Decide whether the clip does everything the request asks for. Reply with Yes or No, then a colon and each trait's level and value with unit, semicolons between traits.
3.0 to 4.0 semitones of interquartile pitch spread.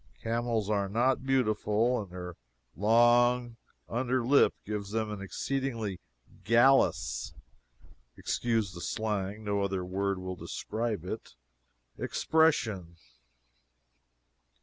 Yes: average, 3.5 semitones